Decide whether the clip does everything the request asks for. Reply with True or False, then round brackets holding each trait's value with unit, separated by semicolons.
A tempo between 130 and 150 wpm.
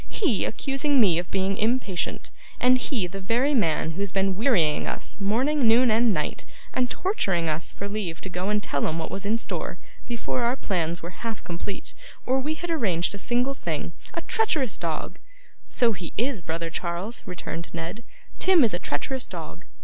False (190 wpm)